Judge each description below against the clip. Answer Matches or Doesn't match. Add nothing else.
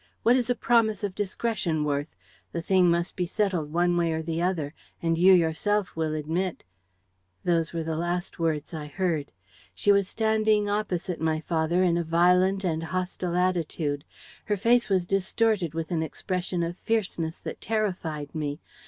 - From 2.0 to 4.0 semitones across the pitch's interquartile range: Matches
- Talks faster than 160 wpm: Matches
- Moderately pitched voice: Matches